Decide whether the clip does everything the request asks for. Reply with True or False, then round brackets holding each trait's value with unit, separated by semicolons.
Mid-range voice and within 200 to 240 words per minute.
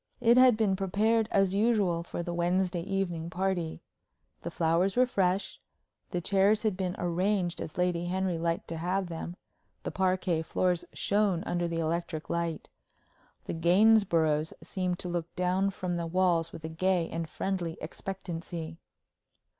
False (180 Hz; 155 wpm)